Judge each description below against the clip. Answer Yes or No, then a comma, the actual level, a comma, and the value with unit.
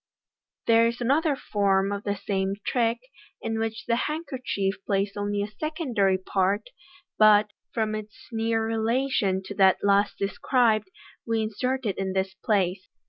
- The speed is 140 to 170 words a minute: Yes, average, 150 wpm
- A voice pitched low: No, high, 215 Hz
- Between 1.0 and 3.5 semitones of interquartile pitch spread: Yes, average, 2.8 semitones